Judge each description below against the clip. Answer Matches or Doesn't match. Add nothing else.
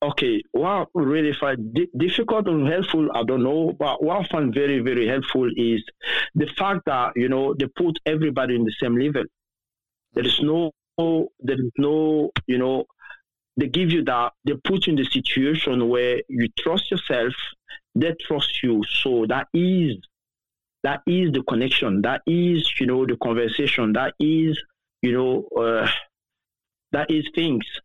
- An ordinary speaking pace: Matches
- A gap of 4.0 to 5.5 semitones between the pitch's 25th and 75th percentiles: Matches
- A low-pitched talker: Doesn't match